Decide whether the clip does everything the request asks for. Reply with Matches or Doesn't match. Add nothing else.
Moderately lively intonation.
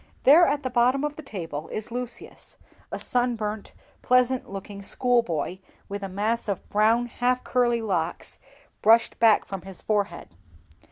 Matches